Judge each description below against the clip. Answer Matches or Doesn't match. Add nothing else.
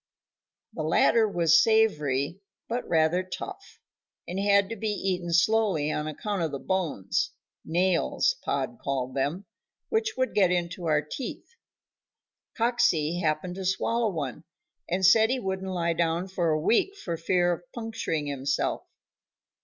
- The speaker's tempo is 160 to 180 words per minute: Doesn't match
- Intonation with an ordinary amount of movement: Matches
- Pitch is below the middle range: Doesn't match